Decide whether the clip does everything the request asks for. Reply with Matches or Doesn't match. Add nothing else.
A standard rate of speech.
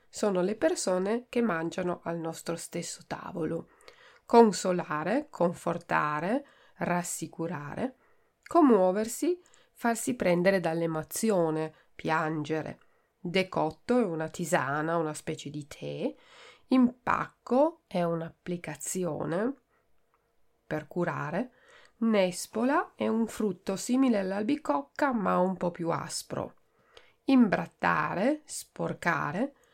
Doesn't match